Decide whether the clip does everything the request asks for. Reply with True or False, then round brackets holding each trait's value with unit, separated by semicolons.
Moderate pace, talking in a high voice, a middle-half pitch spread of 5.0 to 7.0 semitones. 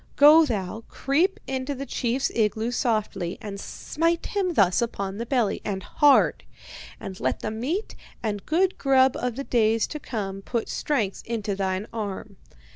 True (160 wpm; 230 Hz; 5.3 semitones)